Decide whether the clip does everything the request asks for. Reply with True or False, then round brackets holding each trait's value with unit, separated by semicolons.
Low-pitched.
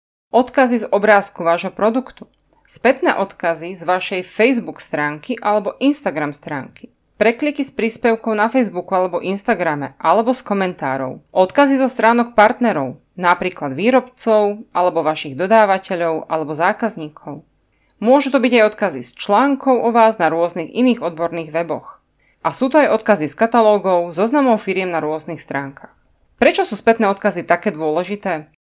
False (200 Hz)